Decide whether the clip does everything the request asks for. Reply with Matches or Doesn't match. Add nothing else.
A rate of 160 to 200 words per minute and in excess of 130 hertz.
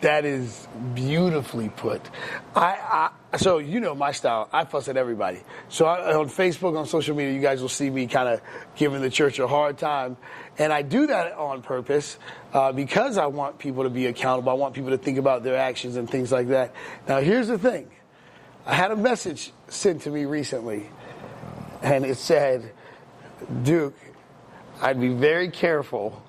Matches